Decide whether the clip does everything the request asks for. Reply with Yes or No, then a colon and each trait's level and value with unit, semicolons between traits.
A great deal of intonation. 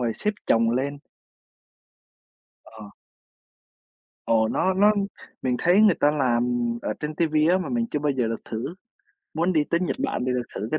Yes: wide, 7.1 semitones